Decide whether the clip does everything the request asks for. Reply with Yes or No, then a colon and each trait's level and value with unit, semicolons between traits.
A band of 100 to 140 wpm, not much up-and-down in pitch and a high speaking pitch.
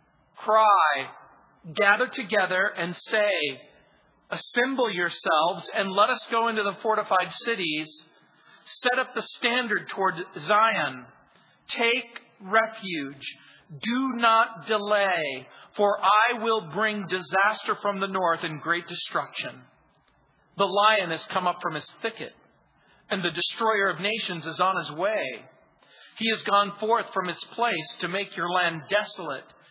No: slow, 135 wpm; average, 4.3 semitones; high, 200 Hz